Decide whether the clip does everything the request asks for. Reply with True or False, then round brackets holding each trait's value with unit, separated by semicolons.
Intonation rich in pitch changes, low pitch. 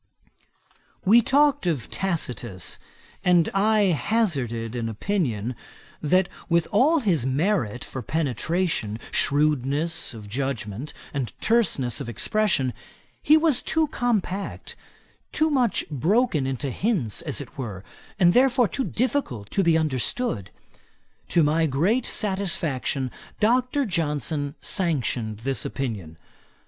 False (8.9 semitones; 160 Hz)